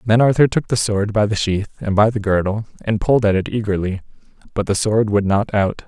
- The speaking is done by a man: Yes, male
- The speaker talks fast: Yes, fast, 235 wpm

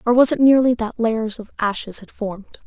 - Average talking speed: No, fast, 225 wpm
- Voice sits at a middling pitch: No, high, 230 Hz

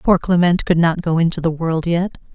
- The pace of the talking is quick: Yes, fast, 230 wpm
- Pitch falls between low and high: Yes, medium, 170 Hz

